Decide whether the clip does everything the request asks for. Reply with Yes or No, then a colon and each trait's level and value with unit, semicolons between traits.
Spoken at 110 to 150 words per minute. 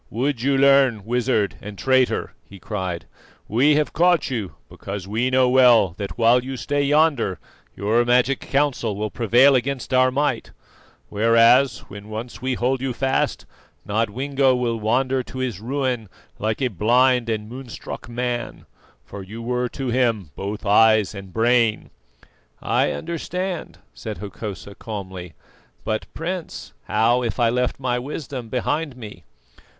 Yes: average, 145 wpm